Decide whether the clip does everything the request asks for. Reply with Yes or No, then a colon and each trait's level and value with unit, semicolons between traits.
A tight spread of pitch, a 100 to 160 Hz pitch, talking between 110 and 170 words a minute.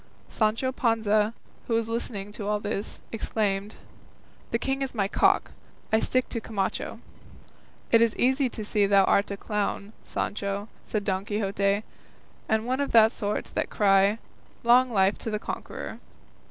No: narrow, 2.3 semitones; high, 215 Hz; average, 155 wpm